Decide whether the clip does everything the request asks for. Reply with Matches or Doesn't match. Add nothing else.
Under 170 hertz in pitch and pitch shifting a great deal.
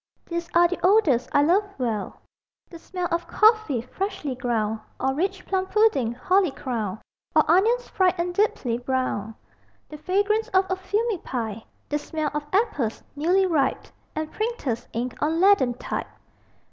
Doesn't match